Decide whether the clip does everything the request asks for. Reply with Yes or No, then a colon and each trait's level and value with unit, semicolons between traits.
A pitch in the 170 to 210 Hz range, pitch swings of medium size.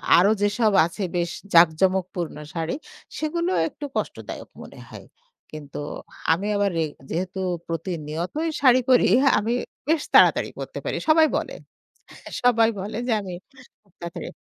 No: high, 190 Hz; wide, 6.4 semitones